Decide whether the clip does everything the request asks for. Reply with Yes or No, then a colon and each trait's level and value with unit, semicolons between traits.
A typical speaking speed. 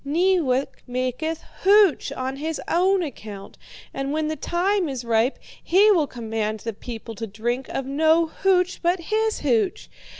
Yes: average, 155 wpm